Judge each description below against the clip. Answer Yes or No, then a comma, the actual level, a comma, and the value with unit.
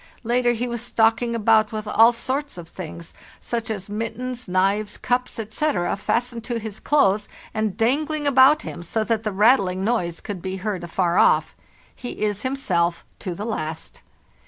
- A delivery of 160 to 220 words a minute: Yes, average, 165 wpm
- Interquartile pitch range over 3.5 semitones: Yes, average, 4.0 semitones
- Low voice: No, high, 220 Hz